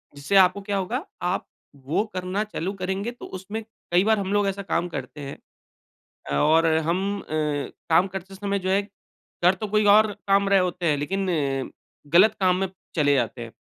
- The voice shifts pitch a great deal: No, average, 3.5 semitones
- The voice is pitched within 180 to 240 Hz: Yes, high, 190 Hz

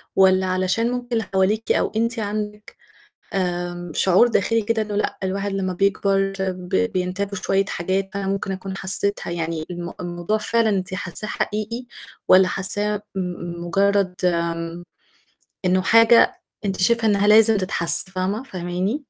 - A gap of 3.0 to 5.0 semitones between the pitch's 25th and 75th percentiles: No, narrow, 2.5 semitones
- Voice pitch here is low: No, high, 195 Hz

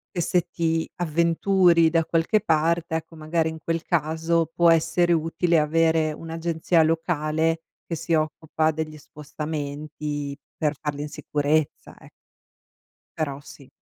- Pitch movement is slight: Yes, narrow, 1.5 semitones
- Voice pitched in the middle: Yes, medium, 160 Hz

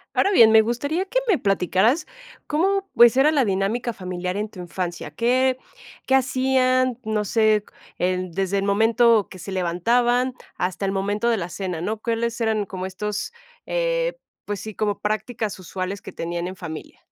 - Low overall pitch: No, high, 215 Hz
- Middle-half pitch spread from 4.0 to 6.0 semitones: Yes, average, 4.7 semitones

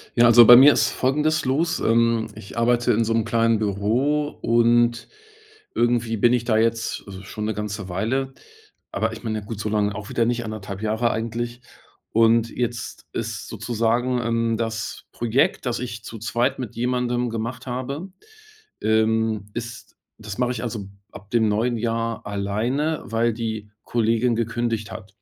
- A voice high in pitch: No, low, 115 Hz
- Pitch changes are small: Yes, narrow, 1.8 semitones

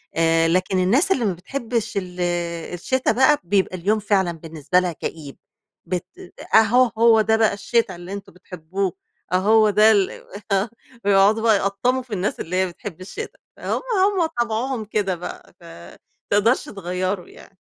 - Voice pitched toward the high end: Yes, high, 200 Hz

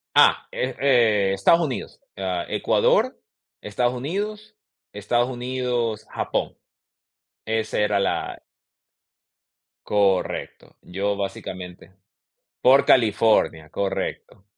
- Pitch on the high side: No, low, 110 Hz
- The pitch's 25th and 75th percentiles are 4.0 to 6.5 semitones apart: Yes, average, 4.5 semitones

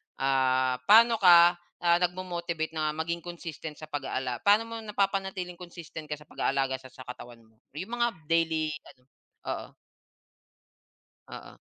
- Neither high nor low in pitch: Yes, medium, 165 Hz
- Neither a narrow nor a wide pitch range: Yes, average, 5.0 semitones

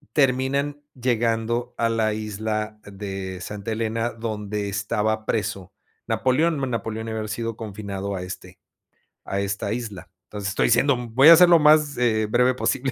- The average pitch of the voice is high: No, low, 110 Hz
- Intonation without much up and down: No, average, 3.0 semitones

